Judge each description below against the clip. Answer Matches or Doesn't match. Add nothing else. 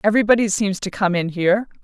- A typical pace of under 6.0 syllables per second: Doesn't match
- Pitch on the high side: Matches